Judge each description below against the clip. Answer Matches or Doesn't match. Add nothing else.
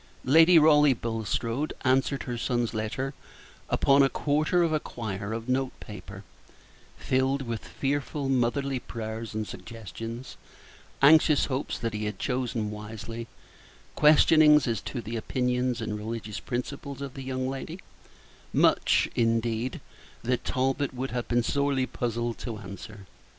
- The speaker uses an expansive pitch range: Doesn't match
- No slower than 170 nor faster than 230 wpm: Doesn't match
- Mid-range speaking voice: Doesn't match